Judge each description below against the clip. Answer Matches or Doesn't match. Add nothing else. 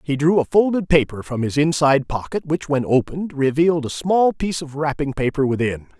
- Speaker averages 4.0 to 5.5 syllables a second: Doesn't match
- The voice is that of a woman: Doesn't match